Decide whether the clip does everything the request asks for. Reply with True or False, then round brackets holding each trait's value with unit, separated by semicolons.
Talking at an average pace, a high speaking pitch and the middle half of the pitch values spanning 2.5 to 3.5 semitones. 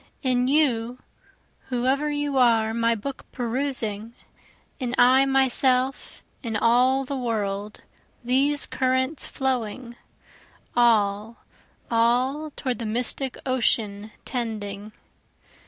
False (95 wpm; 245 Hz; 2.8 semitones)